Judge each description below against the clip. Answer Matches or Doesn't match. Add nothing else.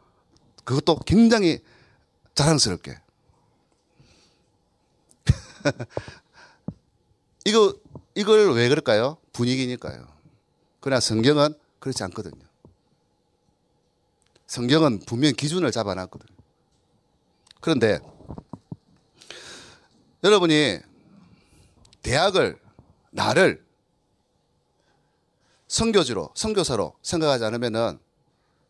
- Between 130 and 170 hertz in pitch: Matches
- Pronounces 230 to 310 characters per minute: Doesn't match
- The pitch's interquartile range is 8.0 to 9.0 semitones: Doesn't match